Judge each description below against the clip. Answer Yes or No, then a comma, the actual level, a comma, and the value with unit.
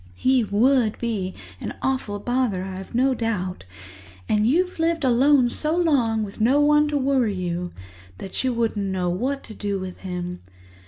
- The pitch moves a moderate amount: No, wide, 5.7 semitones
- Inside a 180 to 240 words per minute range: No, average, 165 wpm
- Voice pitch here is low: No, high, 230 Hz